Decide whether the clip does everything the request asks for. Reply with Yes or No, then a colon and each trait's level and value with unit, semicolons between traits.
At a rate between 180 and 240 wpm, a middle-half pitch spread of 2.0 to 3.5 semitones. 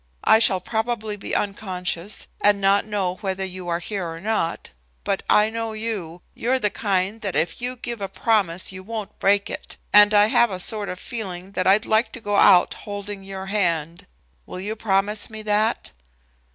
Yes: average, 190 wpm; narrow, 2.6 semitones